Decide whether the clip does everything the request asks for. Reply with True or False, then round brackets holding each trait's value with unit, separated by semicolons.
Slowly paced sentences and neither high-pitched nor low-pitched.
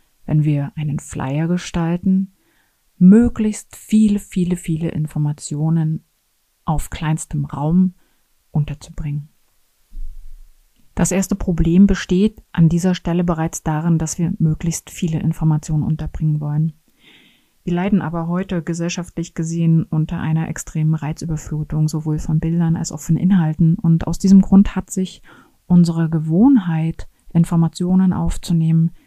True (120 wpm; 165 Hz)